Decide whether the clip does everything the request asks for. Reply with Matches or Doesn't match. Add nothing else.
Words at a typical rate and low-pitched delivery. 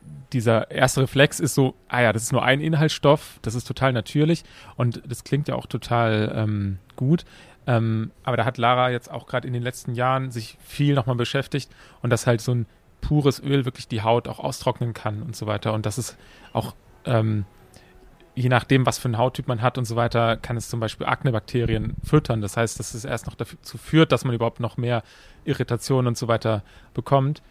Doesn't match